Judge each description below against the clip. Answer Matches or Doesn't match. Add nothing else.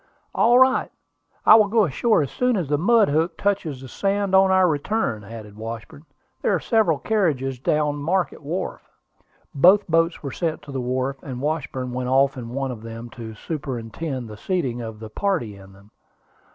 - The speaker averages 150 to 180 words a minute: Doesn't match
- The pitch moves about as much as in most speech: Doesn't match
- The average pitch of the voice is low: Doesn't match